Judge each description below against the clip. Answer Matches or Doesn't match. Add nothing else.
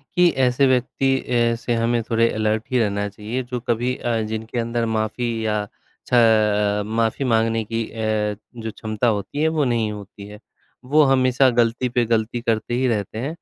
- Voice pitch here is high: Doesn't match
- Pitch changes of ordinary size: Doesn't match